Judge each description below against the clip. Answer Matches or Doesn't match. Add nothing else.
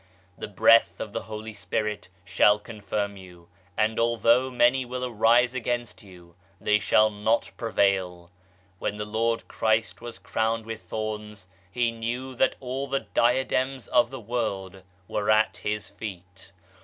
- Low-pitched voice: Matches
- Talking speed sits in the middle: Matches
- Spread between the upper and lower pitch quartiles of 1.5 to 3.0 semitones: Matches